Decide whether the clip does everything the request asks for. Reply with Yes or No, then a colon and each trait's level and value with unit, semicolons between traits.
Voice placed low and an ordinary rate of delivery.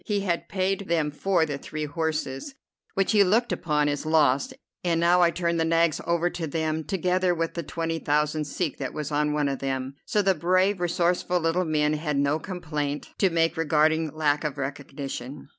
No: medium, 160 Hz; average, 195 wpm